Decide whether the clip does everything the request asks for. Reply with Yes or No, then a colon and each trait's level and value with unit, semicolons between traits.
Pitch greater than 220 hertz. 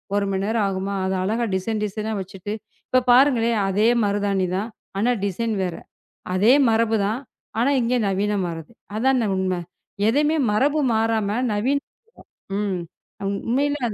No: high, 215 Hz